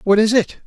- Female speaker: No, male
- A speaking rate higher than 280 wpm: No, fast, 270 wpm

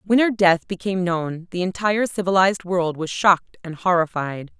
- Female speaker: Yes, female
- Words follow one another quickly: No, average, 170 wpm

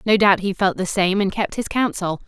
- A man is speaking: No, female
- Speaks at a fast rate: Yes, fast, 265 wpm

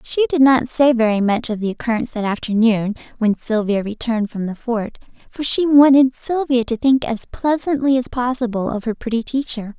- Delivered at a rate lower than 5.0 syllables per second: No, 5.3 syllables/s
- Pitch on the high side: Yes, high, 240 Hz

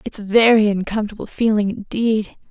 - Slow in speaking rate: Yes, slow, 120 wpm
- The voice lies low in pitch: No, high, 210 Hz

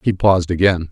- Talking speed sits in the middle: Yes, average, 195 wpm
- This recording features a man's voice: Yes, male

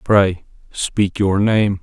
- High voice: No, low, 100 Hz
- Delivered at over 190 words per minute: No, slow, 130 wpm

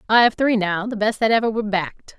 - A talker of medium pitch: No, high, 215 Hz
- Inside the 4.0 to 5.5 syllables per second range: No, 6.5 syllables/s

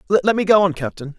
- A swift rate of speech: Yes, fast, 255 wpm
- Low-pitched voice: No, medium, 185 Hz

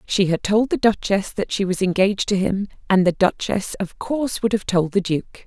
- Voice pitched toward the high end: Yes, high, 200 Hz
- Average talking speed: No, fast, 230 wpm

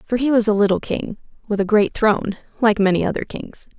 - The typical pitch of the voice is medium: No, high, 215 Hz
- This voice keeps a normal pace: No, fast, 220 wpm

